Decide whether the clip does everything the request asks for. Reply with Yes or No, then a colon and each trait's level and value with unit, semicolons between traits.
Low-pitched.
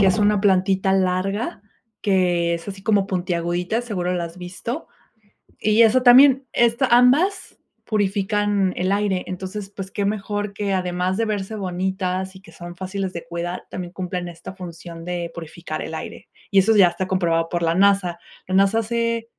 No: high, 190 Hz